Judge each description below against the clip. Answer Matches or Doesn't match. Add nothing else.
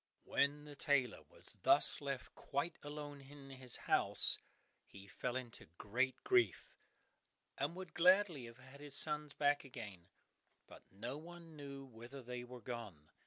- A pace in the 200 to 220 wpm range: Doesn't match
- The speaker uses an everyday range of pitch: Matches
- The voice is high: Doesn't match